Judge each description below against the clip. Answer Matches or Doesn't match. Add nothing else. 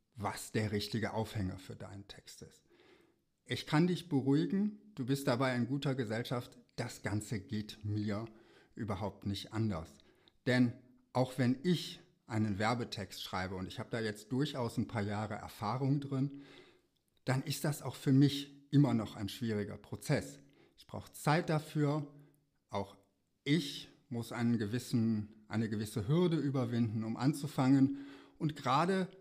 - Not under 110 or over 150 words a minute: Matches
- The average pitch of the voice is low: Matches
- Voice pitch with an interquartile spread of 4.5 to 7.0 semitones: Matches